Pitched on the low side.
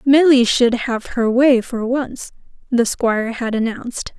No: high, 245 Hz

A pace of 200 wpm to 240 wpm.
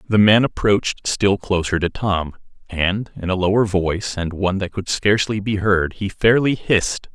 No: average, 185 wpm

